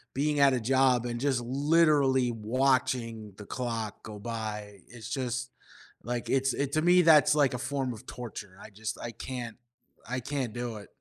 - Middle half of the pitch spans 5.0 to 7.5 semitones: No, average, 3.1 semitones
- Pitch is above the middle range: No, low, 125 Hz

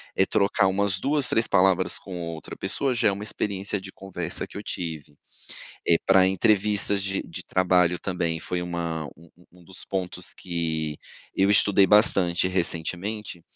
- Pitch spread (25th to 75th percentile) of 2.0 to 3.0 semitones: Yes, narrow, 2.5 semitones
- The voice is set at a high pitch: No, very low, 95 Hz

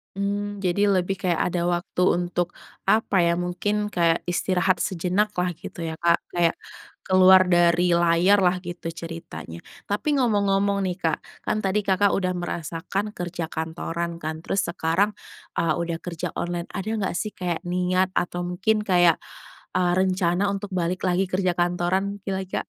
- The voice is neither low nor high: Yes, medium, 180 Hz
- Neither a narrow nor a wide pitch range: No, narrow, 2.1 semitones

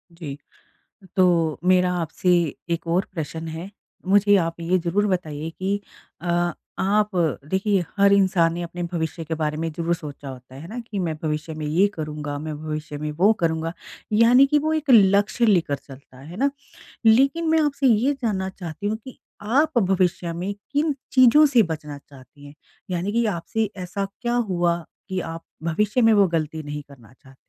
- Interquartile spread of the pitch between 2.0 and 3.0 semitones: No, average, 4.8 semitones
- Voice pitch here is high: No, medium, 180 Hz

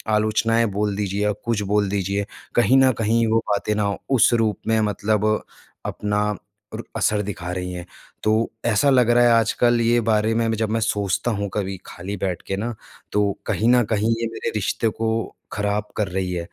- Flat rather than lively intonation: Yes, narrow, 2.1 semitones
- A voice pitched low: Yes, low, 105 Hz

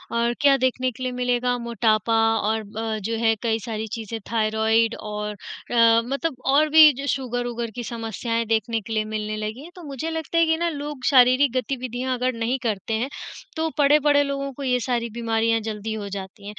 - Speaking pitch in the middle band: No, high, 235 Hz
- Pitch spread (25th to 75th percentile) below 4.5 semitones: Yes, average, 3.3 semitones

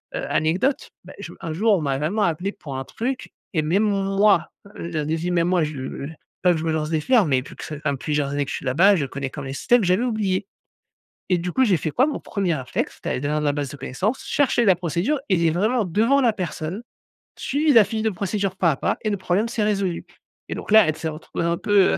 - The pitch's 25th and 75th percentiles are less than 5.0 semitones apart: No, wide, 5.4 semitones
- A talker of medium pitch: Yes, medium, 180 Hz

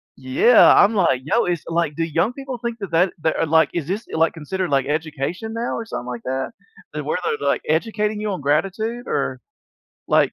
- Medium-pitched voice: Yes, medium, 175 Hz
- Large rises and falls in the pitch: Yes, wide, 6.5 semitones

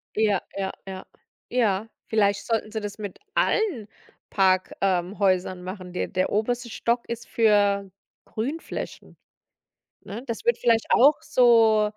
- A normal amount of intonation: Yes, average, 3.2 semitones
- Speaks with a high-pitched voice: Yes, high, 215 Hz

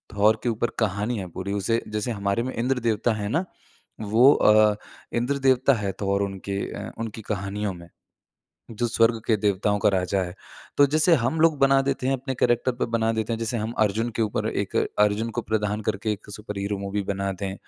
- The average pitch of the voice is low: Yes, low, 110 Hz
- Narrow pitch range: No, average, 3.1 semitones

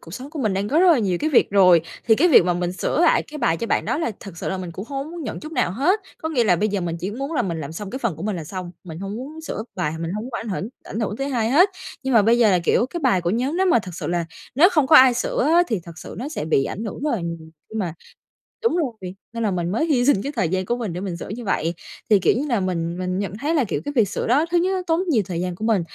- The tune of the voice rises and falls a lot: Yes, wide, 7.1 semitones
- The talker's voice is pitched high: Yes, high, 215 Hz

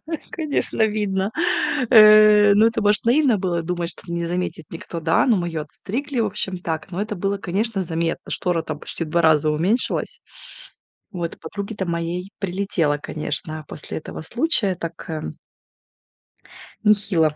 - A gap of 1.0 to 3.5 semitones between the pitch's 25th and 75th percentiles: No, average, 4.1 semitones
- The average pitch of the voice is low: No, medium, 185 Hz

